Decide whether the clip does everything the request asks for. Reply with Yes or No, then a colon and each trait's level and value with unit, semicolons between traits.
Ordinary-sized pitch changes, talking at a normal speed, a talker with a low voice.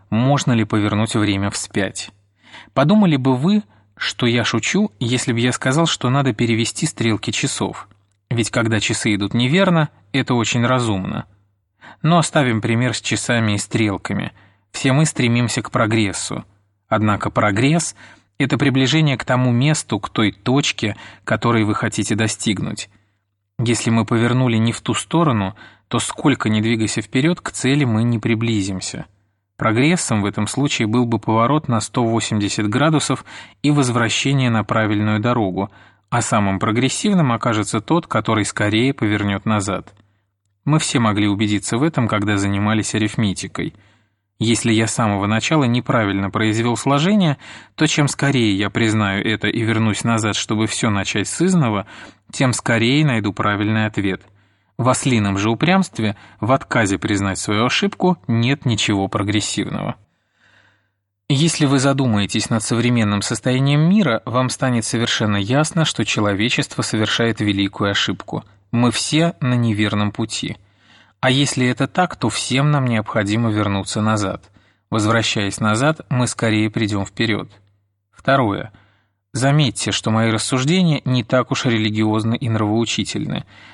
Yes: average, 3.8 semitones; average, 135 wpm; low, 115 Hz